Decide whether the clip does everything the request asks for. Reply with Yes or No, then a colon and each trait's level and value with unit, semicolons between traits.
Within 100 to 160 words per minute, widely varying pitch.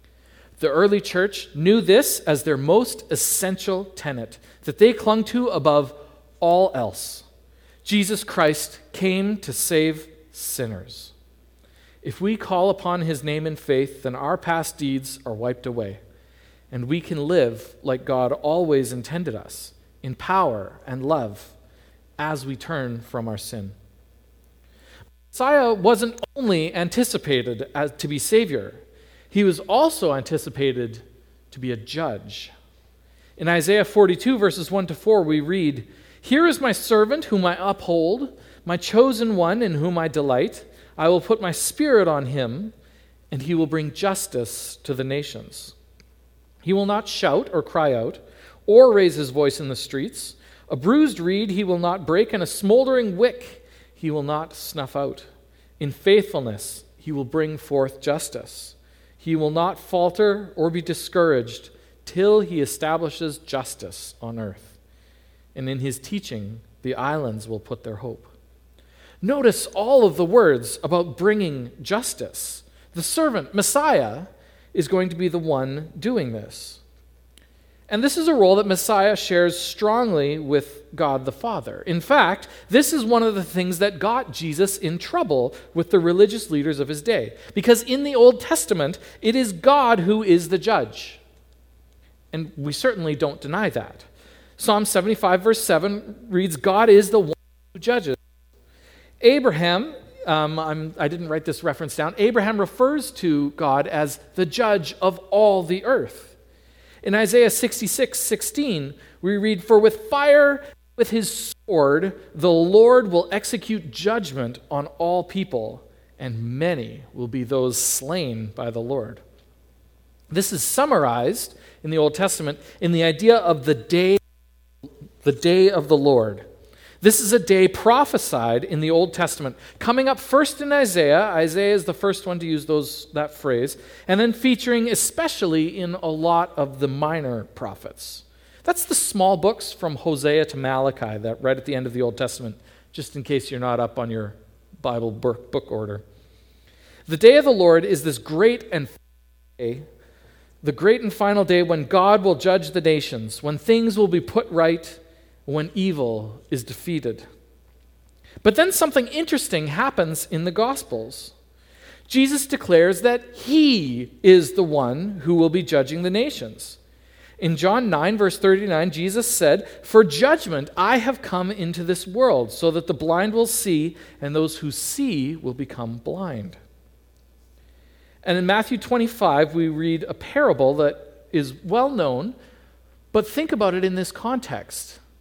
Yes: average, 155 wpm; wide, 8.0 semitones